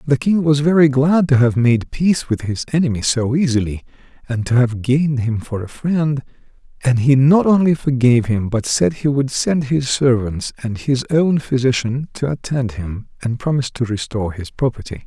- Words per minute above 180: Yes, average, 190 wpm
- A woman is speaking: No, male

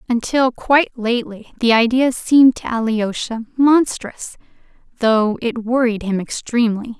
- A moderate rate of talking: No, slow, 120 wpm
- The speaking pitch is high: Yes, high, 235 Hz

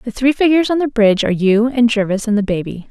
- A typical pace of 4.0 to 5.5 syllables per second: No, 6.8 syllables/s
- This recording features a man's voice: No, female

